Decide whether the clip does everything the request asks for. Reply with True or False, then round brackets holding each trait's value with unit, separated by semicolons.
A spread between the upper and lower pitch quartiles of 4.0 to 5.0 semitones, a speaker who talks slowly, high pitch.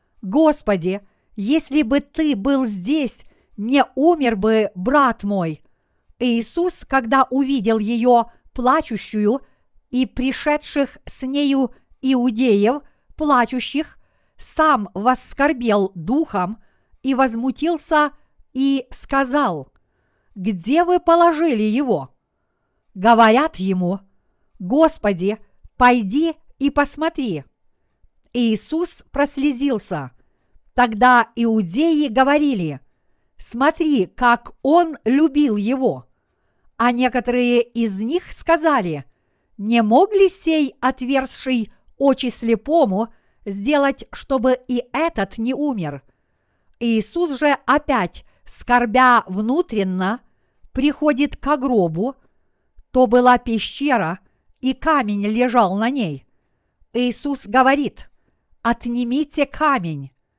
True (4.7 semitones; 85 wpm; 250 Hz)